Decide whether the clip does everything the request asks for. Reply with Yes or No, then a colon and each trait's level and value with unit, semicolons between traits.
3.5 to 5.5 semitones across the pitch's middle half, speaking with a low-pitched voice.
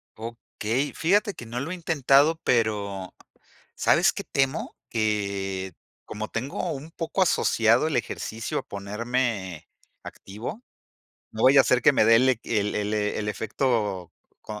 Yes: average, 4.6 semitones; low, 115 Hz